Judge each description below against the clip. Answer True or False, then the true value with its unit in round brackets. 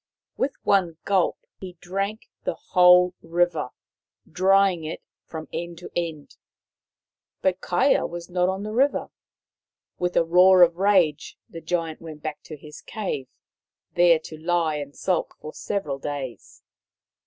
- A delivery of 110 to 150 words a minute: True (140 wpm)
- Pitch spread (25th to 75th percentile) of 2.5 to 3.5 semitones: True (2.8 semitones)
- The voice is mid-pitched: True (175 Hz)